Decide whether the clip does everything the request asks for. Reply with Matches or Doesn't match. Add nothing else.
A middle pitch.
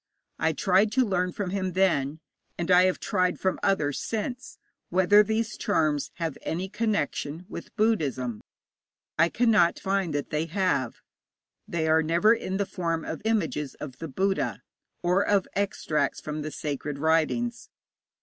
Matches